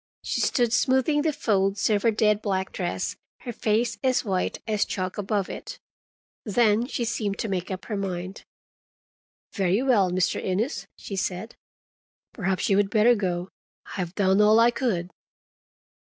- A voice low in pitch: No, high, 205 Hz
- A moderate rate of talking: Yes, average, 160 wpm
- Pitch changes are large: No, average, 3.4 semitones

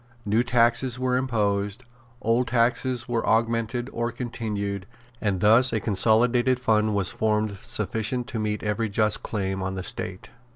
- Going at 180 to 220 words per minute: No, average, 150 wpm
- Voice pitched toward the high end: No, low, 110 Hz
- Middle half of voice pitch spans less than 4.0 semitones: Yes, narrow, 2.5 semitones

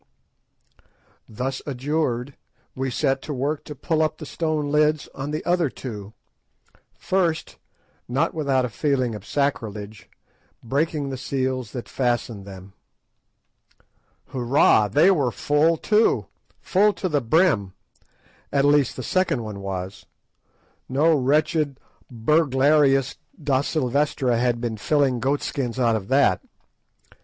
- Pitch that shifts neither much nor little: Yes, average, 4.0 semitones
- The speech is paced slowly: Yes, slow, 120 wpm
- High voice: No, low, 135 Hz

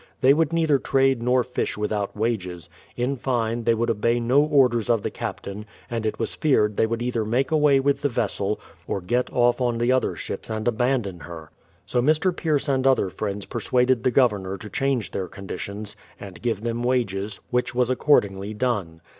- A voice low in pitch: Yes, low, 120 Hz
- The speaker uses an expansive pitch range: No, average, 3.8 semitones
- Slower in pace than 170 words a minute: No, average, 190 wpm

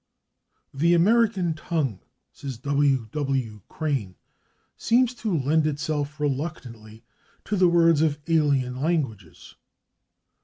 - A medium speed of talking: No, slow, 105 wpm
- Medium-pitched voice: Yes, medium, 150 Hz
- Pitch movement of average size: Yes, average, 4.1 semitones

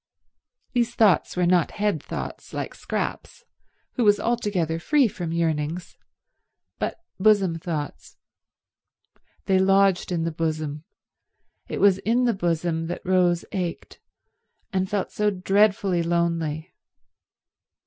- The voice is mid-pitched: Yes, medium, 180 Hz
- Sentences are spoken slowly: Yes, slow, 120 wpm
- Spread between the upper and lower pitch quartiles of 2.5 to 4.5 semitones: Yes, average, 3.5 semitones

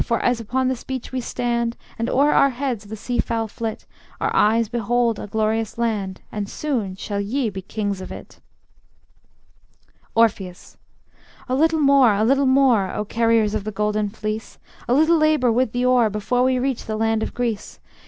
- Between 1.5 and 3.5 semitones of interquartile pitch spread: Yes, average, 3.1 semitones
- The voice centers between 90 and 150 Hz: No, high, 230 Hz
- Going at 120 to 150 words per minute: No, average, 185 wpm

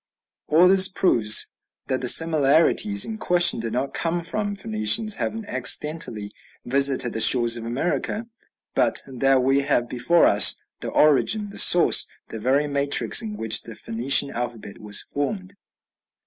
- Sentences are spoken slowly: No, average, 150 wpm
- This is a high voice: No, medium, 140 Hz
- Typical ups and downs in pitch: No, wide, 6.8 semitones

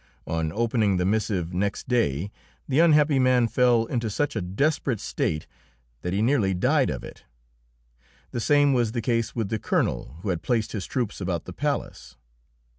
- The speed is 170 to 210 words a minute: Yes, average, 175 wpm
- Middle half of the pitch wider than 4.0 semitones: Yes, average, 4.8 semitones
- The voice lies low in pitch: Yes, low, 110 Hz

